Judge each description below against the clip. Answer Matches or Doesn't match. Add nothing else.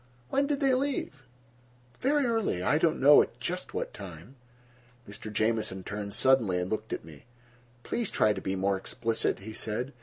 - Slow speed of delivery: Doesn't match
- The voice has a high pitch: Doesn't match